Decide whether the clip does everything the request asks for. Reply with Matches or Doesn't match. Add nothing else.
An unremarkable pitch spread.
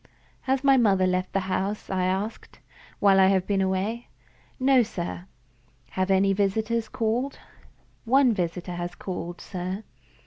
Matches